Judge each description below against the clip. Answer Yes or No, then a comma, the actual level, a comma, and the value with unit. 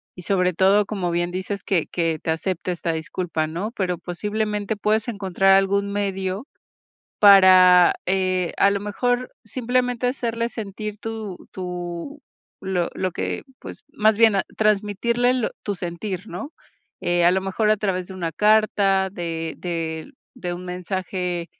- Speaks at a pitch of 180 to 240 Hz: Yes, high, 190 Hz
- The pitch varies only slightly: No, average, 3.0 semitones